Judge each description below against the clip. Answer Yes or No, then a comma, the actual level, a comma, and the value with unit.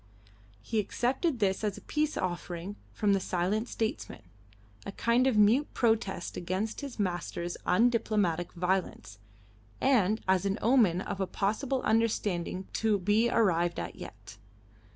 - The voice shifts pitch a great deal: No, average, 4.0 semitones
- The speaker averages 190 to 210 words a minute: No, slow, 135 wpm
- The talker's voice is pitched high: Yes, high, 205 Hz